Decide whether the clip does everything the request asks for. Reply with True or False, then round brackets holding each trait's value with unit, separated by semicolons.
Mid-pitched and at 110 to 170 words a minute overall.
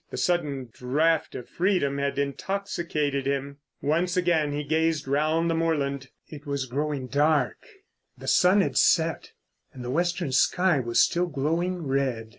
True (150 Hz; 150 wpm)